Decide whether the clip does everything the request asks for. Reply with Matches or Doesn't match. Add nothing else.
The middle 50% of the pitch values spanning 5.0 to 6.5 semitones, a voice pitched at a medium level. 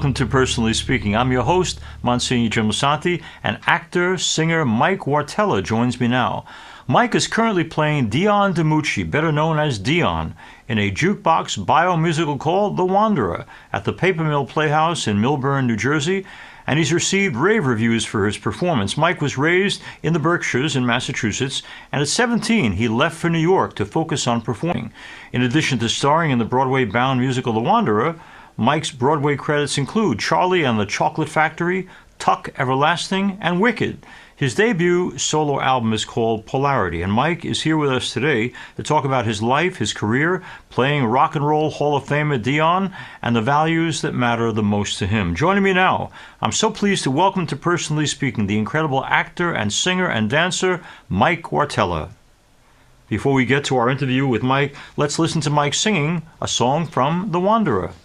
Matches